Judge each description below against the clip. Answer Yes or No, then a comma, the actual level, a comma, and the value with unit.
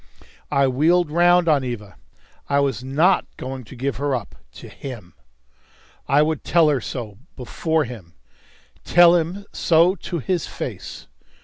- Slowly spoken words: No, average, 145 wpm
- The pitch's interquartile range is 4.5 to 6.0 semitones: Yes, average, 5.0 semitones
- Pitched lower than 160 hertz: Yes, medium, 140 Hz